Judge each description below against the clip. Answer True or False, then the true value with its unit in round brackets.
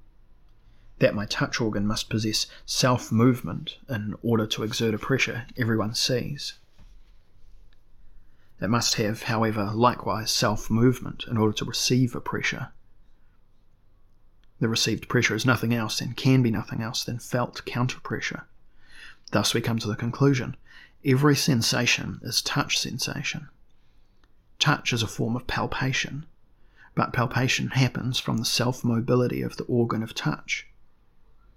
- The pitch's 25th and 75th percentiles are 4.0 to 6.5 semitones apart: False (2.9 semitones)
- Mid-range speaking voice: False (115 Hz)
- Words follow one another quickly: False (140 wpm)